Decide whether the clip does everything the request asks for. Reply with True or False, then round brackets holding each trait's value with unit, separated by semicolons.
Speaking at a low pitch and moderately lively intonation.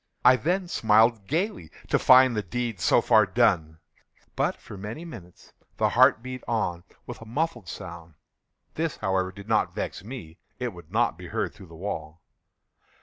False (110 Hz; 5.8 semitones)